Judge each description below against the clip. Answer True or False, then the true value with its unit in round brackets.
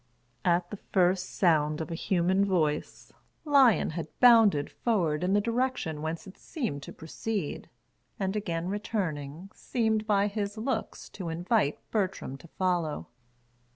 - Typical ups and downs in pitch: True (4.7 semitones)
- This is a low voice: False (185 Hz)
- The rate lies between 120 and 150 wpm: True (140 wpm)